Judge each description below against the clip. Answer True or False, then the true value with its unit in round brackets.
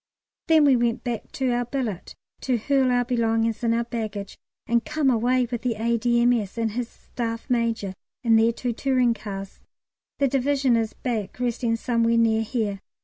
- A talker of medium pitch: False (235 Hz)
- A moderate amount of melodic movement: False (1.7 semitones)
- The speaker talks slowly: False (170 wpm)